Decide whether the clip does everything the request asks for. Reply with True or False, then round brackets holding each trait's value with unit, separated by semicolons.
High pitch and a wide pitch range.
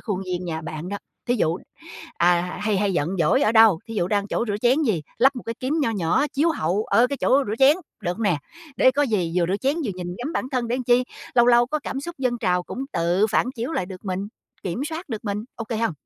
True (220 Hz; 5.9 semitones)